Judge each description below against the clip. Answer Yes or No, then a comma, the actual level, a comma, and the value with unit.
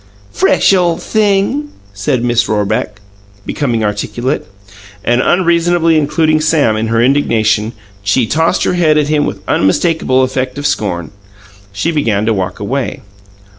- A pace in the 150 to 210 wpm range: No, average, 140 wpm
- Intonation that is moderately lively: No, wide, 6.9 semitones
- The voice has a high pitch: No, low, 130 Hz